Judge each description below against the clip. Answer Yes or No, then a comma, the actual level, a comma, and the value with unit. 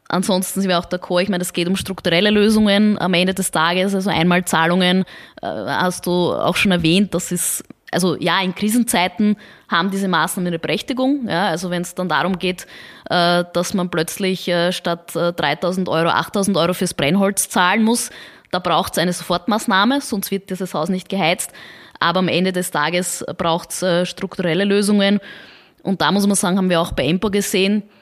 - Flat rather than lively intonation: Yes, narrow, 2.3 semitones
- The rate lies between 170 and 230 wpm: Yes, average, 180 wpm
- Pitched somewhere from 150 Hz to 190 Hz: Yes, medium, 185 Hz